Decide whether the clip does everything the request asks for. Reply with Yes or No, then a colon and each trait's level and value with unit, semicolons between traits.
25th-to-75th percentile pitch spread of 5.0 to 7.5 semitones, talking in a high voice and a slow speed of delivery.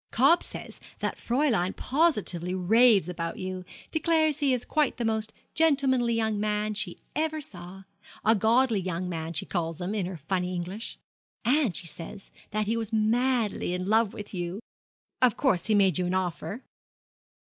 No: average, 5.3 semitones; high, 210 Hz; average, 165 wpm